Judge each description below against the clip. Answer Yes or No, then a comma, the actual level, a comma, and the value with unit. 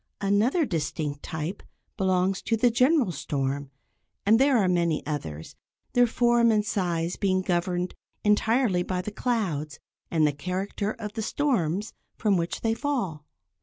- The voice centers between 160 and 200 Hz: Yes, high, 190 Hz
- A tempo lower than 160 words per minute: Yes, average, 145 wpm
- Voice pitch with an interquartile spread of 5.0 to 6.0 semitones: Yes, average, 5.3 semitones